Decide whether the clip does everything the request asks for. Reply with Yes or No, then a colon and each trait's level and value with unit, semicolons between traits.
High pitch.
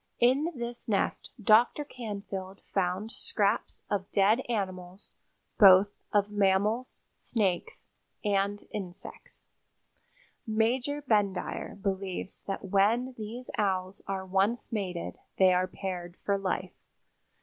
Yes: high, 200 Hz